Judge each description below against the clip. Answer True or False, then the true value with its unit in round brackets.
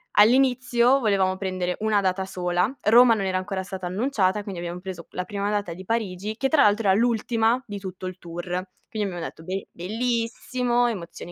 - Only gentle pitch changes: False (3.9 semitones)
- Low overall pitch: False (200 Hz)